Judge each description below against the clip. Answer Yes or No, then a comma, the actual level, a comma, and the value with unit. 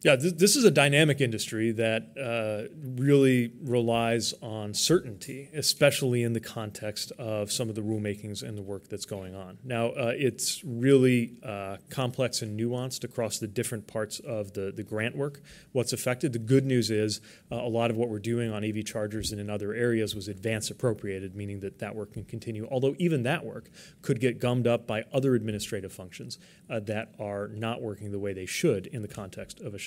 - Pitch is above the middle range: No, low, 115 Hz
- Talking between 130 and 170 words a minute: No, average, 200 wpm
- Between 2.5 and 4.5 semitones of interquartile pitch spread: Yes, average, 3.3 semitones